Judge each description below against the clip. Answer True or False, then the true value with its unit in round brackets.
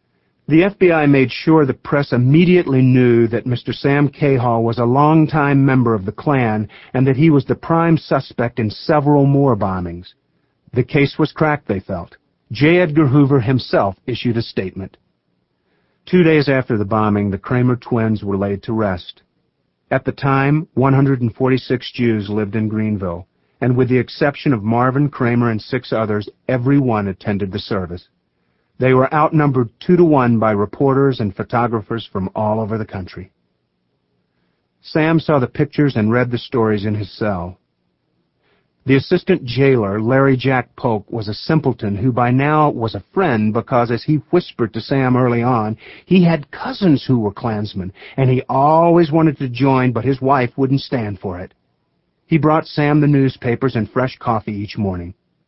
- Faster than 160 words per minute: True (170 wpm)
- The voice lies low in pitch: True (125 Hz)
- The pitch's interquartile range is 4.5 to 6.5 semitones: True (4.8 semitones)